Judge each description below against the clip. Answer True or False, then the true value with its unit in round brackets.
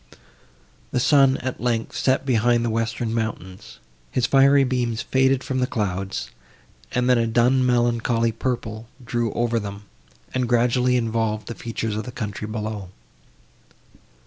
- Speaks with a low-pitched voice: True (120 Hz)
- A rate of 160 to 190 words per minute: False (145 wpm)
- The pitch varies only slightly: True (2.1 semitones)